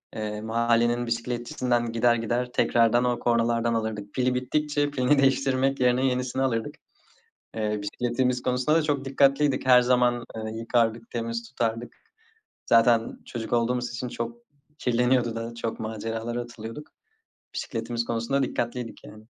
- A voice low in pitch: Yes, low, 120 Hz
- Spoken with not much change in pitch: Yes, narrow, 1.7 semitones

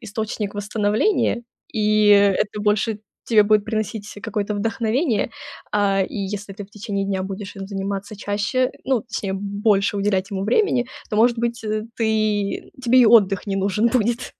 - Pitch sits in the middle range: No, high, 210 Hz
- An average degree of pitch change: No, narrow, 2.0 semitones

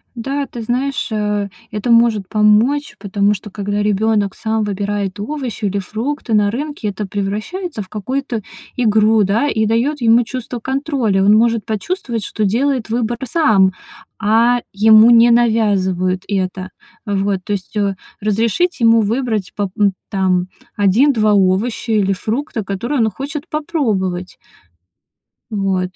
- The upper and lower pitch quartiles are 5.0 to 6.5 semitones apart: No, average, 3.1 semitones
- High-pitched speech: Yes, high, 215 Hz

